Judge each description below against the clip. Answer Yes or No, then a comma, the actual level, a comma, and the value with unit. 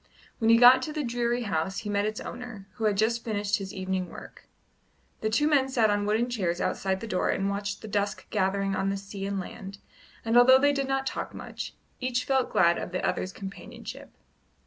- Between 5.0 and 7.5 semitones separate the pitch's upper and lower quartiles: No, average, 3.7 semitones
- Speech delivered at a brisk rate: Yes, fast, 210 wpm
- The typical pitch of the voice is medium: No, high, 210 Hz